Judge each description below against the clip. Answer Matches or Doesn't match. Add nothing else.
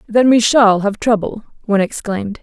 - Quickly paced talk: Doesn't match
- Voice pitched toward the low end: Doesn't match